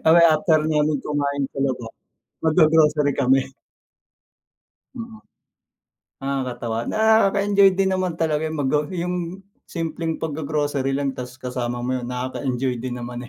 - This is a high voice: No, medium, 150 Hz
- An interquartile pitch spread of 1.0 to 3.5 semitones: No, average, 4.2 semitones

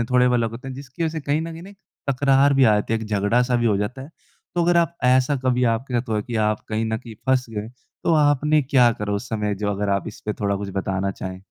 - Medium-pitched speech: No, low, 120 Hz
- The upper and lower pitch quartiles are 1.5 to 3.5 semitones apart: No, average, 4.5 semitones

